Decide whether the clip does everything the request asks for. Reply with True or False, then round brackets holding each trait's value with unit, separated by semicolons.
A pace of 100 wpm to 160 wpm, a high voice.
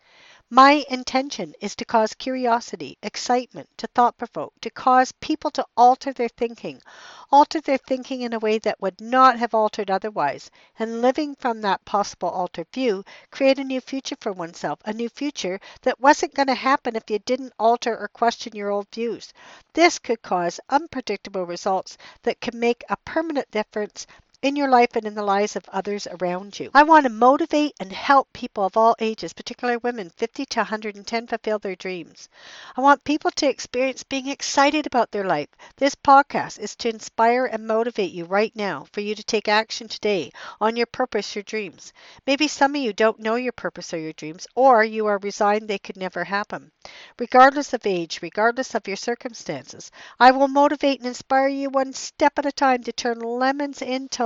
False (190 wpm; 235 Hz)